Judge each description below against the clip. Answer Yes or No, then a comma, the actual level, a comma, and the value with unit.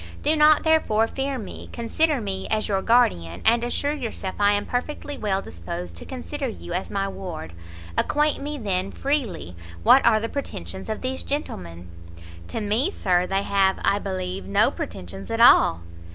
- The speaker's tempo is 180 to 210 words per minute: No, average, 170 wpm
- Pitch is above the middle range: Yes, high, 205 Hz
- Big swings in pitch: Yes, wide, 6.7 semitones